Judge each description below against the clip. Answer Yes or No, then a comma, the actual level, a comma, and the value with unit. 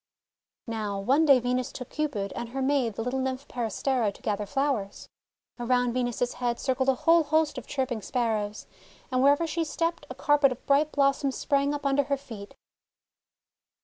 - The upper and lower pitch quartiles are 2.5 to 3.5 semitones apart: Yes, average, 3.2 semitones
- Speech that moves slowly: No, average, 180 wpm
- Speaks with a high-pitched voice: Yes, very high, 260 Hz